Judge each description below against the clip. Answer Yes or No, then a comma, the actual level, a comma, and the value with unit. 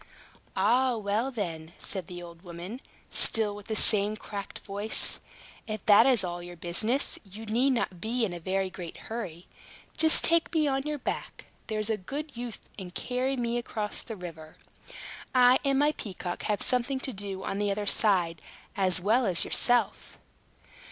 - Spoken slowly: No, average, 170 wpm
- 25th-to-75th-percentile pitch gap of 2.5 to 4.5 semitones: No, average, 4.9 semitones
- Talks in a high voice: Yes, high, 210 Hz